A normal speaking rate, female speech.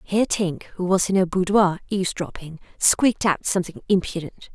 Yes: average, 160 wpm; female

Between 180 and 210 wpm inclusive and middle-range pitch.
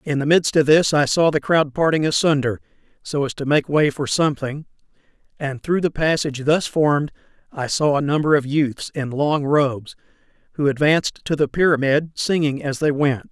Yes: average, 190 wpm; medium, 145 Hz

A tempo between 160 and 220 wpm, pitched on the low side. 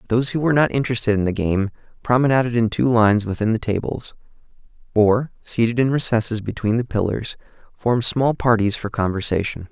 Yes: average, 165 wpm; low, 115 Hz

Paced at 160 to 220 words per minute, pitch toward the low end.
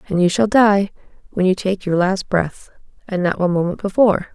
No: fast, 205 wpm; high, 190 Hz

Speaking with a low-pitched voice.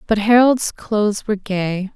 No: high, 210 Hz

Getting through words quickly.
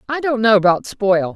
Yes: fast, 220 wpm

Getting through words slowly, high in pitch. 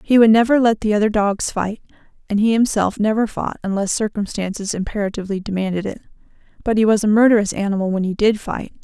No: average, 190 wpm; high, 210 Hz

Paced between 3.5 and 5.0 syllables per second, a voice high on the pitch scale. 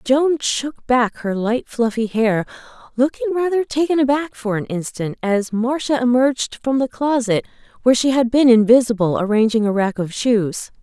Yes: 4.8 syllables/s; high, 240 Hz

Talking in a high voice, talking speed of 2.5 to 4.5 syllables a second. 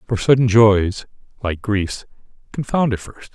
No: low, 110 Hz; 4.2 syllables/s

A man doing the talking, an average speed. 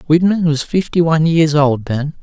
Yes: male; average, 190 wpm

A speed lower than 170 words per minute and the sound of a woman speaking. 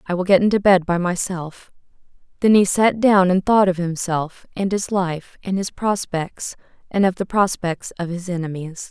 No: average, 180 wpm; female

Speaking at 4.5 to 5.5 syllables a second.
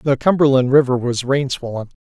Yes: 5.4 syllables/s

